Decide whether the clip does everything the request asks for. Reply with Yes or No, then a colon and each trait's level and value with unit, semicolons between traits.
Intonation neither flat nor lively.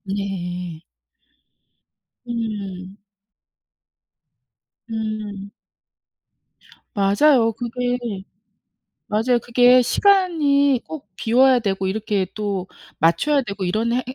Yes: average, 4.1 semitones